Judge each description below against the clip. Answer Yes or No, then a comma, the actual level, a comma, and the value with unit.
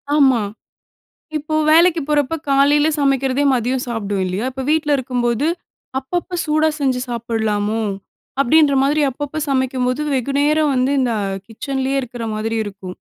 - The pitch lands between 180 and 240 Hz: No, very high, 265 Hz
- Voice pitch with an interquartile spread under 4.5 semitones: Yes, average, 3.6 semitones